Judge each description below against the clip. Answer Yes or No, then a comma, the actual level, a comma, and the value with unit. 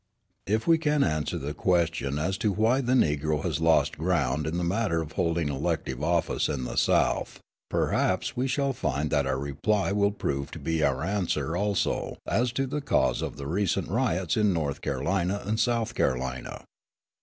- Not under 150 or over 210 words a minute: Yes, average, 180 wpm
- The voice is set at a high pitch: No, very low, 85 Hz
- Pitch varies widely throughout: Yes, wide, 6.3 semitones